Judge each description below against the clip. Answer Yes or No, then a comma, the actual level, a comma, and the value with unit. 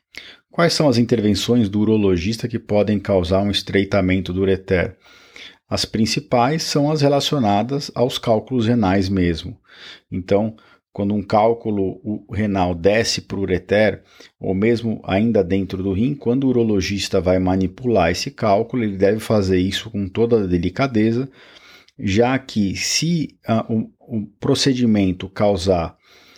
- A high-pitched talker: No, low, 105 Hz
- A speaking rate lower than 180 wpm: Yes, average, 140 wpm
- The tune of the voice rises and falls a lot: No, average, 3.7 semitones